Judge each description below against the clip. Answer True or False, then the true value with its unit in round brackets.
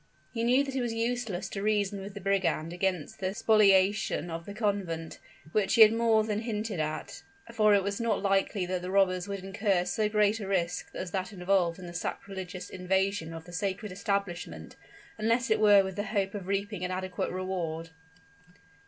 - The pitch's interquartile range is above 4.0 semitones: False (2.6 semitones)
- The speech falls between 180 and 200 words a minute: True (190 wpm)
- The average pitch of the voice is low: False (195 Hz)